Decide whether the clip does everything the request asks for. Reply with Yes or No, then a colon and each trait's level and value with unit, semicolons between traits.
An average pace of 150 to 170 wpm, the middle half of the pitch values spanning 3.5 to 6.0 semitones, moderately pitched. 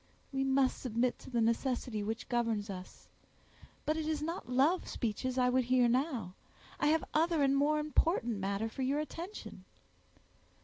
No: average, 165 wpm; average, 4.6 semitones; very high, 255 Hz